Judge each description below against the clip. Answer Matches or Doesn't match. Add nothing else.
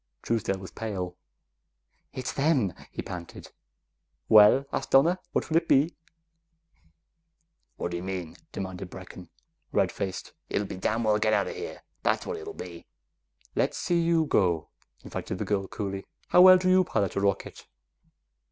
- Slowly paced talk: Doesn't match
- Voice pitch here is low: Matches